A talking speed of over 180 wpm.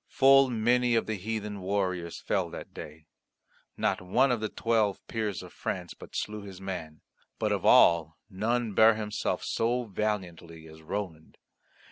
No: average, 155 wpm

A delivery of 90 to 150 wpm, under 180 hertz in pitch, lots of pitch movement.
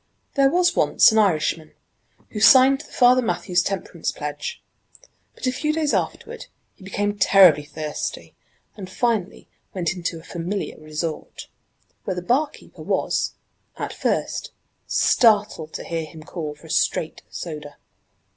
No: average, 140 wpm; high, 190 Hz; wide, 7.0 semitones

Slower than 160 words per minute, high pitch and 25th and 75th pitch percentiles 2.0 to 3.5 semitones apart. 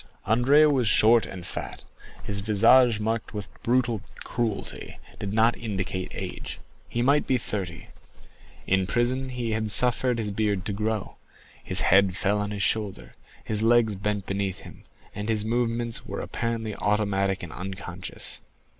No: average, 150 wpm; low, 110 Hz; average, 3.0 semitones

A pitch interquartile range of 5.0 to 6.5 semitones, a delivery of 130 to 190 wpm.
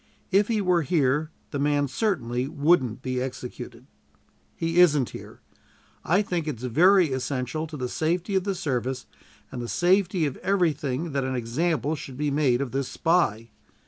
Yes: average, 5.3 semitones; average, 165 wpm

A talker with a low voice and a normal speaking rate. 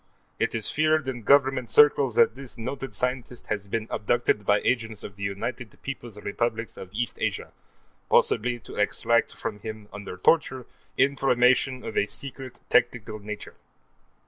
Yes: low, 120 Hz; average, 150 wpm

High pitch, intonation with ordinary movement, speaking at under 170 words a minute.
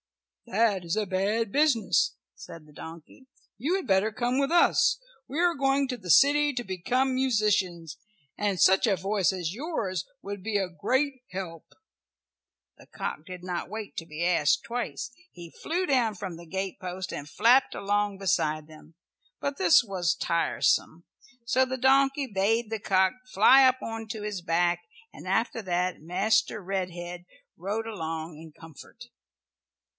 No: high, 200 Hz; wide, 5.7 semitones; average, 160 wpm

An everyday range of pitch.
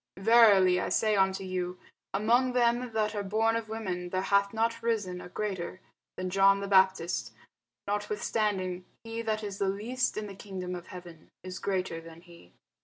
Yes: average, 3.1 semitones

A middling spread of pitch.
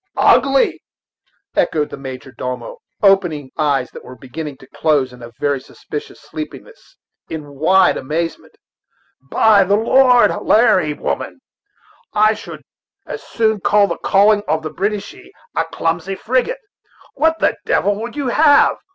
No: wide, 7.0 semitones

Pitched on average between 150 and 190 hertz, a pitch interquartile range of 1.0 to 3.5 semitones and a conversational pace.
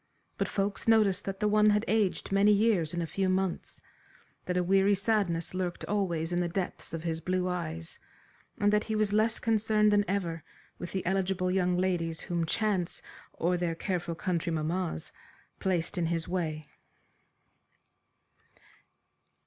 Yes: medium, 185 Hz; average, 3.1 semitones; average, 155 wpm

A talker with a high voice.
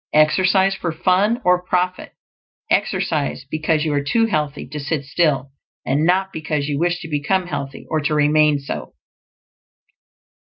No: medium, 155 Hz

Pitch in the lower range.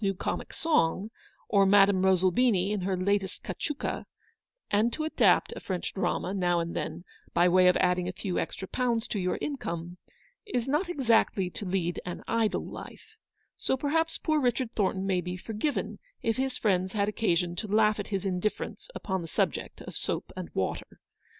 No: high, 195 Hz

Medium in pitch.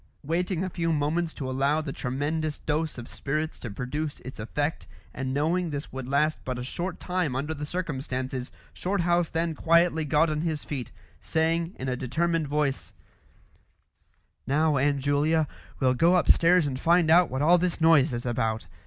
Yes: medium, 150 Hz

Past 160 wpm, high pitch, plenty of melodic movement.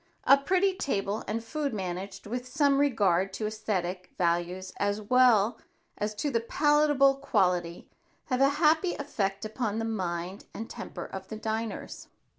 No: average, 150 wpm; high, 220 Hz; wide, 6.1 semitones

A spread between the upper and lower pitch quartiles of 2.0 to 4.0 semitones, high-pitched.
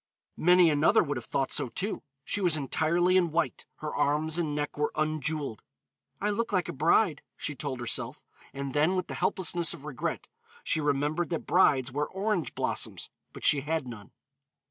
No: average, 3.4 semitones; medium, 155 Hz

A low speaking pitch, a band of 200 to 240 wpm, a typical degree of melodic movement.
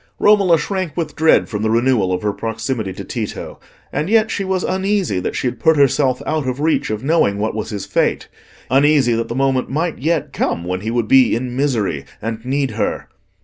No: low, 130 Hz; fast, 205 wpm; wide, 6.1 semitones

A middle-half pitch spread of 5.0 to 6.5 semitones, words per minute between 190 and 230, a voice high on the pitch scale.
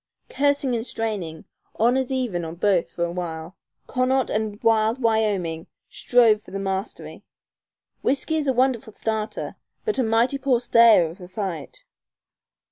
No: wide, 5.4 semitones; average, 145 wpm; high, 220 Hz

